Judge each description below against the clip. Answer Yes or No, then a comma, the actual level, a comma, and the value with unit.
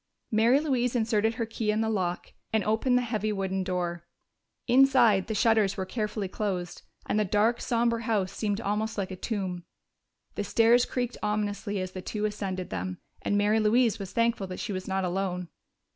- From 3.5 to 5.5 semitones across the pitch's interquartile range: No, average, 3.0 semitones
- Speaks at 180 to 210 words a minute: Yes, average, 185 wpm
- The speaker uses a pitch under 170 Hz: No, high, 210 Hz